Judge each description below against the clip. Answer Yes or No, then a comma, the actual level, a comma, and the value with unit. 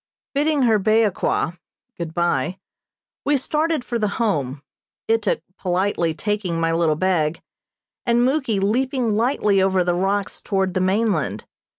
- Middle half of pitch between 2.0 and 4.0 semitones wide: No, average, 4.9 semitones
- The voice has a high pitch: Yes, high, 195 Hz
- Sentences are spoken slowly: Yes, slow, 130 wpm